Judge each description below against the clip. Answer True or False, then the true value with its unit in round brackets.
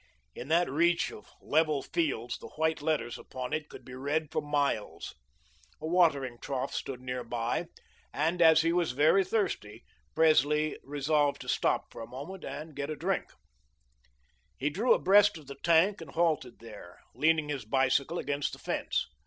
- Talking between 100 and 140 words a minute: False (170 wpm)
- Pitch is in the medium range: True (150 Hz)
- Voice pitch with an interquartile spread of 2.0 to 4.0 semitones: True (3.6 semitones)